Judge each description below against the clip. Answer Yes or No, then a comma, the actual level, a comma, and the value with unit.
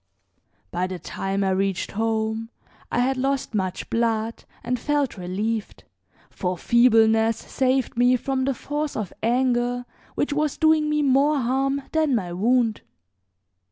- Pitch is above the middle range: Yes, high, 240 Hz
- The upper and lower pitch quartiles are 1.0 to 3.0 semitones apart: No, average, 3.7 semitones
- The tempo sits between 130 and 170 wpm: Yes, average, 140 wpm